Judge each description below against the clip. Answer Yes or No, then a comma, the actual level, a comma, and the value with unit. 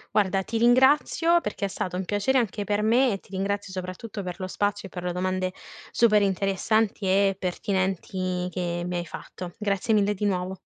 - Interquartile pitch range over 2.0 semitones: Yes, narrow, 2.4 semitones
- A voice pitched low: No, high, 195 Hz